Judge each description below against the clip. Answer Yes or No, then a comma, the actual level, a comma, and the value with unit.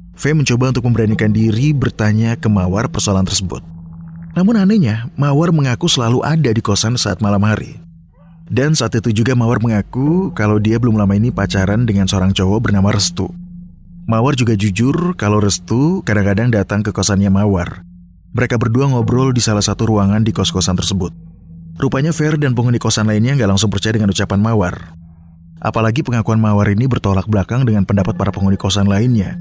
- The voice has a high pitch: No, low, 110 Hz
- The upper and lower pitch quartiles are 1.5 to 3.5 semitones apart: No, average, 4.1 semitones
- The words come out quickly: Yes, fast, 165 wpm